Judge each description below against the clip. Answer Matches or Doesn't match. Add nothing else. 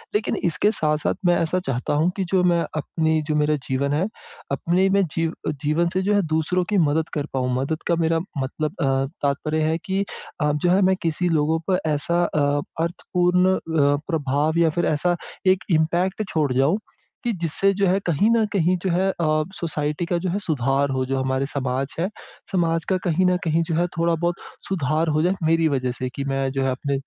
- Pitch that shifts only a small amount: Doesn't match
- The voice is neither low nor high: Matches